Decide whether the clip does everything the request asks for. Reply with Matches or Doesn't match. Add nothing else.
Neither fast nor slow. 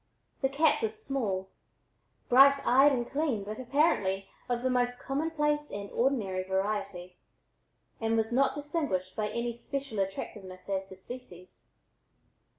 Doesn't match